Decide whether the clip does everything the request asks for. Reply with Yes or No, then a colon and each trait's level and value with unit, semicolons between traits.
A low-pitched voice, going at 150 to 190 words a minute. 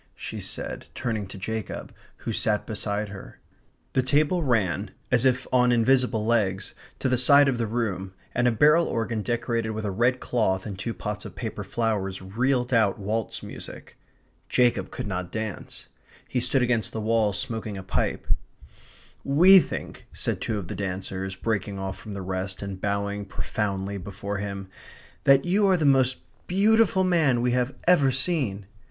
Yes: low, 110 Hz; average, 170 wpm